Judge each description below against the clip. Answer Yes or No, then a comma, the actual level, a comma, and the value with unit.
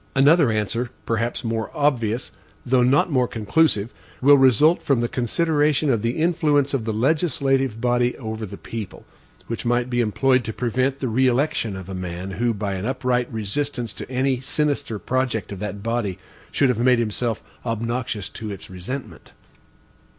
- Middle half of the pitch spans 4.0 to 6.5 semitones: No, average, 3.5 semitones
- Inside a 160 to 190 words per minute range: Yes, average, 165 wpm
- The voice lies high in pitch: No, low, 120 Hz